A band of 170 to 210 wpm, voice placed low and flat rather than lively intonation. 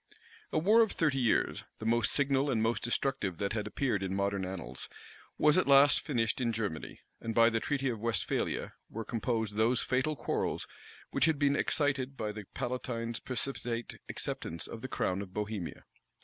No: average, 175 wpm; low, 115 Hz; average, 4.3 semitones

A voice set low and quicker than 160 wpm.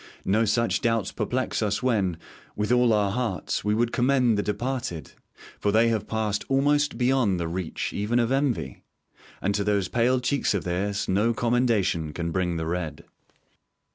Yes: low, 105 Hz; average, 170 wpm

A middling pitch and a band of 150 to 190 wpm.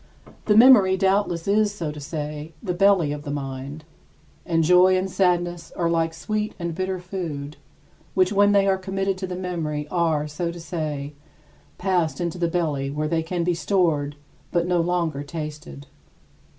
Yes: medium, 170 Hz; average, 170 wpm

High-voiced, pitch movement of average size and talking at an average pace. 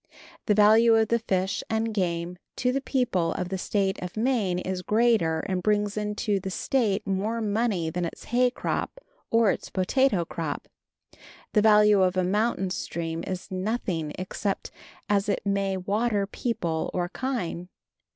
Yes: high, 200 Hz; average, 3.5 semitones; average, 160 wpm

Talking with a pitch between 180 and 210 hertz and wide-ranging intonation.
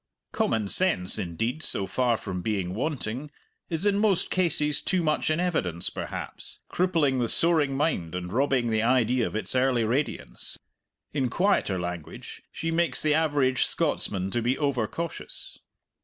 No: low, 130 Hz; wide, 6.7 semitones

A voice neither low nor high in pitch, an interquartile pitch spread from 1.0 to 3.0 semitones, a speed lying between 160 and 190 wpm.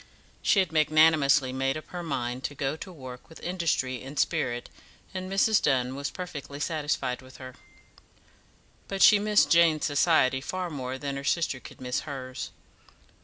No: medium, 145 Hz; average, 4.4 semitones; average, 165 wpm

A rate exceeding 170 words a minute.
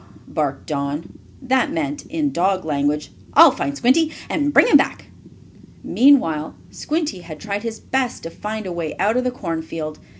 No: average, 165 wpm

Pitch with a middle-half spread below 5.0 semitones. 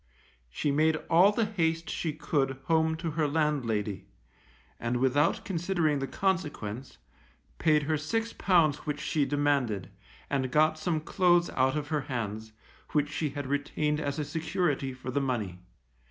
Yes: average, 3.4 semitones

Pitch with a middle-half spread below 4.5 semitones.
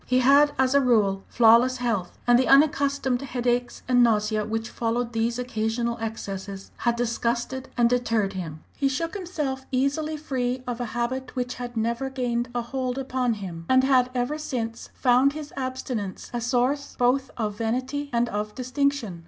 Yes: narrow, 2.5 semitones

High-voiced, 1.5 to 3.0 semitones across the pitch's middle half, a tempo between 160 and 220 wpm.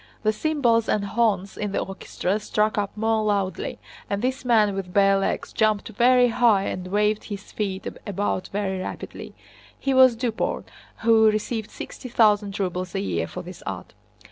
Yes: high, 210 Hz; narrow, 2.5 semitones; average, 170 wpm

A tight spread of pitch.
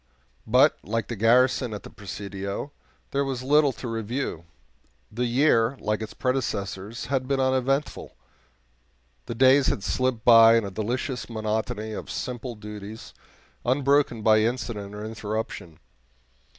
No: average, 3.4 semitones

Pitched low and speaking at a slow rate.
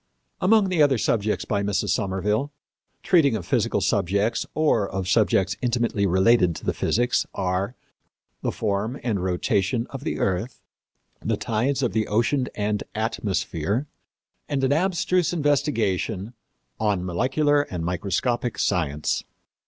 Yes: low, 110 Hz; slow, 130 wpm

